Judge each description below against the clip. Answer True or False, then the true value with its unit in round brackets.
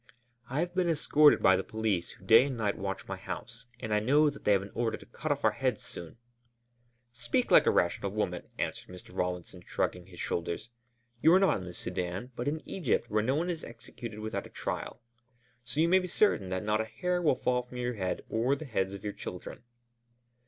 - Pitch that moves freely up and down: True (6.4 semitones)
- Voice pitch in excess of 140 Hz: False (115 Hz)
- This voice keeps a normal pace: False (225 wpm)